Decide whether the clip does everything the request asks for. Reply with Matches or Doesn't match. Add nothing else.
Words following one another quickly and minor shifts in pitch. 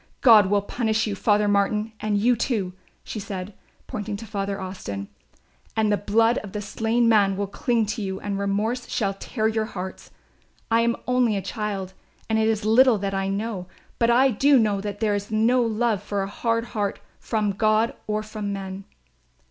Doesn't match